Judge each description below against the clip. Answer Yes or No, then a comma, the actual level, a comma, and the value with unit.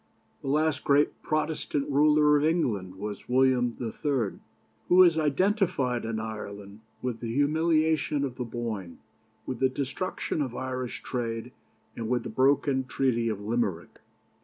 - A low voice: Yes, low, 130 Hz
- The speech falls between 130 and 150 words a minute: Yes, average, 140 wpm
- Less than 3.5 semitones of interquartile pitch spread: No, average, 4.5 semitones